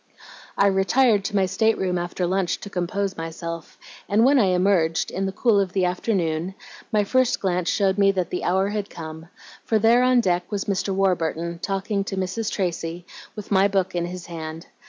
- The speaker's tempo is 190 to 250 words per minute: Yes, average, 195 wpm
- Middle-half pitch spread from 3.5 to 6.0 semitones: No, narrow, 2.4 semitones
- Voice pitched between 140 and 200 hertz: Yes, high, 190 Hz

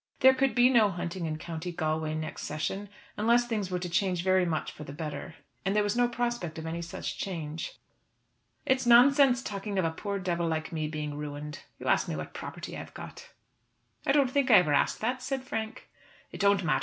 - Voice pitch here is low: No, medium, 185 Hz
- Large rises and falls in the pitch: Yes, wide, 7.0 semitones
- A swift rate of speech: Yes, fast, 215 wpm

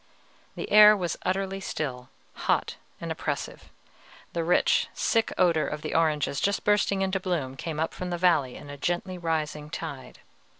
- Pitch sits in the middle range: Yes, medium, 170 Hz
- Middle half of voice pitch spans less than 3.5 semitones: No, average, 3.9 semitones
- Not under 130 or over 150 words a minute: No, average, 165 wpm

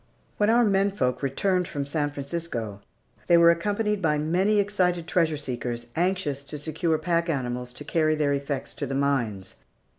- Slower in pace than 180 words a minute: Yes, average, 160 wpm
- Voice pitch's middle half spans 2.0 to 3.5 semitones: No, average, 4.5 semitones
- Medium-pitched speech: Yes, medium, 155 Hz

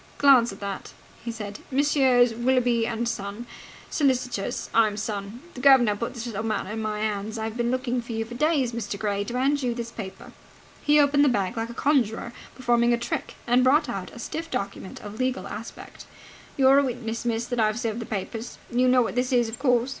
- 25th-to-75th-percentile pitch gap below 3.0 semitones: Yes, narrow, 2.6 semitones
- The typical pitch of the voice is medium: No, high, 235 Hz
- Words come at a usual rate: No, fast, 210 wpm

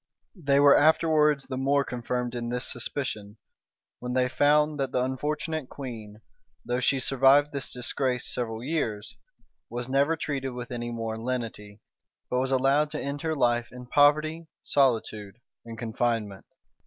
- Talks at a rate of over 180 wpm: No, average, 155 wpm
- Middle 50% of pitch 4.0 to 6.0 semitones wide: No, average, 3.2 semitones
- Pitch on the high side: No, low, 130 Hz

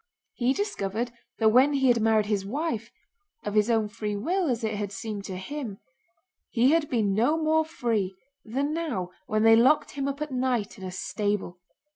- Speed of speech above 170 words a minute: Yes, average, 180 wpm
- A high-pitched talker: Yes, high, 230 Hz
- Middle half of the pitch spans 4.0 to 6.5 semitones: Yes, average, 5.1 semitones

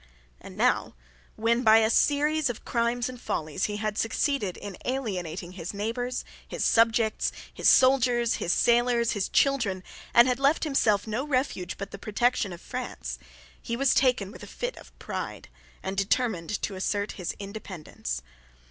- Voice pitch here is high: Yes, high, 225 Hz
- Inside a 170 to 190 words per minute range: No, average, 160 wpm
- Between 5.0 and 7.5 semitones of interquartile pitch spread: No, average, 4.2 semitones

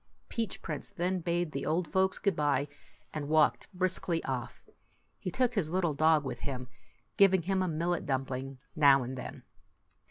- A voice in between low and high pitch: Yes, medium, 160 Hz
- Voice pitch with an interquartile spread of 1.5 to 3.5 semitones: No, average, 4.9 semitones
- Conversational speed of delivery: Yes, average, 165 wpm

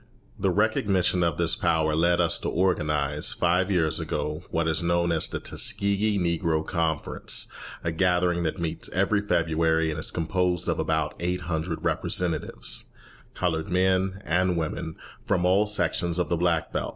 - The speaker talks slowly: No, average, 160 wpm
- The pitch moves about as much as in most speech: No, narrow, 2.2 semitones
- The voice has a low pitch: Yes, very low, 85 Hz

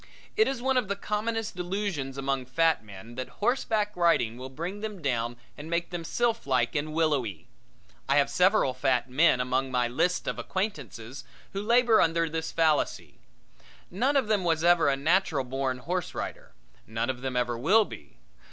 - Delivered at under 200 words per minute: Yes, average, 175 wpm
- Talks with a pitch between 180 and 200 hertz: No, medium, 160 Hz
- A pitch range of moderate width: No, wide, 7.5 semitones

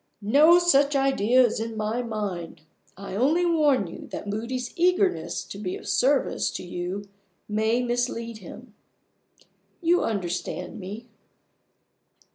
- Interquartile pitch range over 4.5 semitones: Yes, average, 5.1 semitones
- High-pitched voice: Yes, high, 235 Hz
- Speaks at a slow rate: Yes, slow, 125 wpm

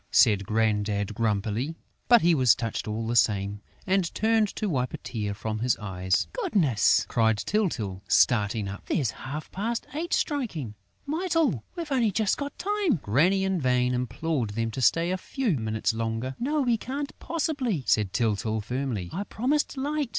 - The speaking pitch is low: Yes, low, 130 Hz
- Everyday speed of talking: Yes, average, 165 wpm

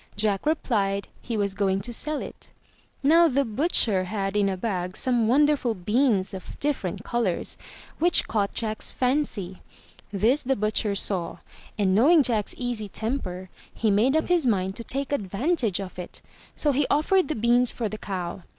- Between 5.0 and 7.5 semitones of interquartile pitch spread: Yes, wide, 5.5 semitones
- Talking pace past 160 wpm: Yes, average, 170 wpm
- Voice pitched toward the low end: No, high, 220 Hz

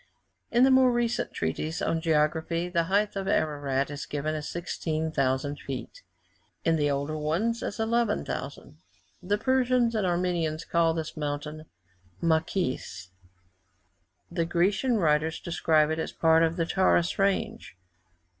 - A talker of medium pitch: Yes, medium, 165 Hz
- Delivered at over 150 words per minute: No, slow, 135 wpm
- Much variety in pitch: No, average, 4.4 semitones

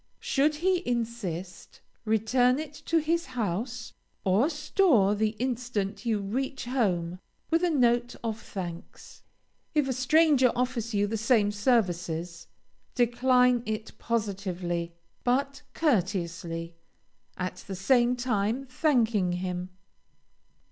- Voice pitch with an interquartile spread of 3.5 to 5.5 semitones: Yes, average, 5.0 semitones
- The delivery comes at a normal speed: No, slow, 115 wpm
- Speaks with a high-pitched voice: Yes, high, 230 Hz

